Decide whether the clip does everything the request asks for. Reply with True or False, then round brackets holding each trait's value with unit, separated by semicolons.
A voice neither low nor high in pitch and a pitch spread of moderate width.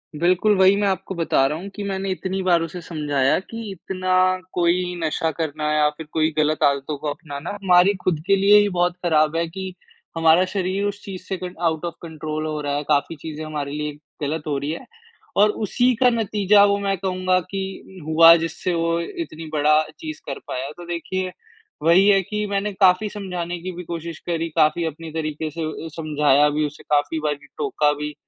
True (170 Hz; 3.7 semitones)